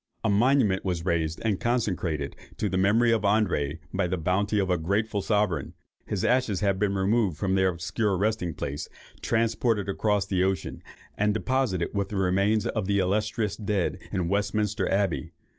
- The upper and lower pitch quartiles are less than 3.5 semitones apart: Yes, narrow, 2.6 semitones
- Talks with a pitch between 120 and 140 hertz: No, low, 100 Hz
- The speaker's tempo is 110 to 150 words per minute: No, average, 170 wpm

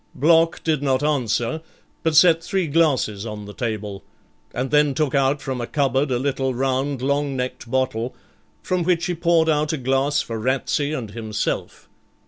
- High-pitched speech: No, low, 135 Hz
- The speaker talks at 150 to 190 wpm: Yes, average, 170 wpm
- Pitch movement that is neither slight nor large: Yes, average, 3.7 semitones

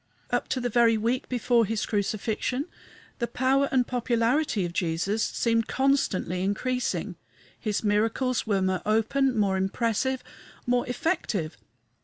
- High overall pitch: Yes, high, 230 Hz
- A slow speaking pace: Yes, slow, 130 wpm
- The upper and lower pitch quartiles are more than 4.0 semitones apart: No, average, 3.6 semitones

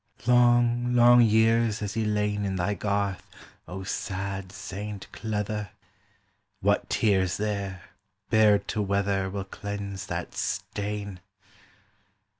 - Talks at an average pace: No, slow, 110 wpm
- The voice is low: Yes, low, 100 Hz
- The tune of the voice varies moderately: No, narrow, 1.7 semitones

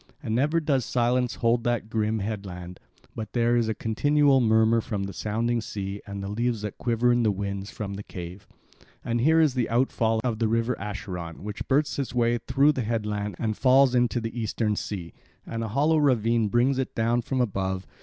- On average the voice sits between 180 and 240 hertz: No, low, 115 Hz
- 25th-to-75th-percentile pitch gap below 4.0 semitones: Yes, average, 2.9 semitones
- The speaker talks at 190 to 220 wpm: Yes, average, 200 wpm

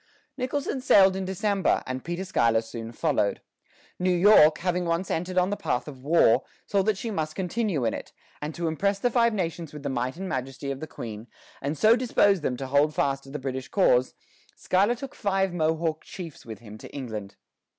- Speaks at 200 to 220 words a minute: Yes, fast, 205 wpm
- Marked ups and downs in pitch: Yes, wide, 6.3 semitones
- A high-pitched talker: No, medium, 165 Hz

